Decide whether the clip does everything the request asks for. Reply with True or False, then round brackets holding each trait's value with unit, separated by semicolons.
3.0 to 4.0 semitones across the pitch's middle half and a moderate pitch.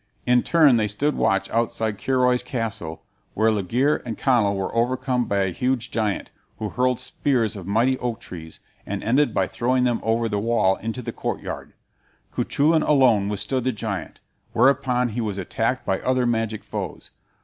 False (3.4 semitones; 115 Hz)